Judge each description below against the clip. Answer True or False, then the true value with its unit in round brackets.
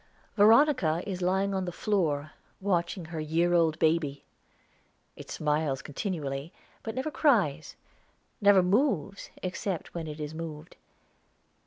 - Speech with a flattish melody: False (4.3 semitones)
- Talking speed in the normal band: False (125 wpm)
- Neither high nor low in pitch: True (170 Hz)